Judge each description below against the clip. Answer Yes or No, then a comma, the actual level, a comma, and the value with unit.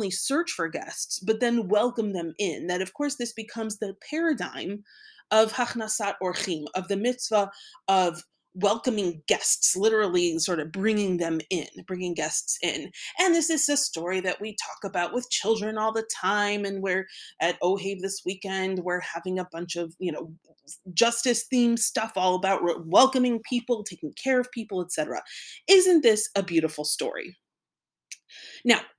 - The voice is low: No, high, 200 Hz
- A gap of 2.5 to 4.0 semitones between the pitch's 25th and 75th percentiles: No, average, 4.9 semitones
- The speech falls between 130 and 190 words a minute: Yes, average, 160 wpm